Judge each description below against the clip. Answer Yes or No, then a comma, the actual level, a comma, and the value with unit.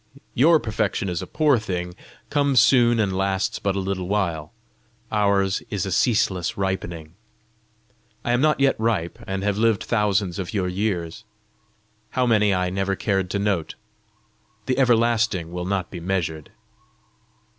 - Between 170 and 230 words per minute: No, average, 150 wpm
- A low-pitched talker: Yes, low, 100 Hz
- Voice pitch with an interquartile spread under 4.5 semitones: Yes, average, 3.8 semitones